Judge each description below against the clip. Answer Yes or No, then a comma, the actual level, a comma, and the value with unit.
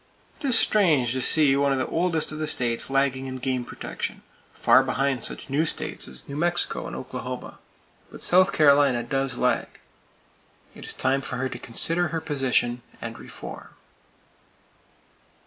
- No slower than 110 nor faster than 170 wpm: Yes, average, 165 wpm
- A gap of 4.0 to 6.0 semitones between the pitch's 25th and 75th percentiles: No, average, 3.3 semitones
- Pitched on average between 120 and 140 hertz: Yes, low, 135 Hz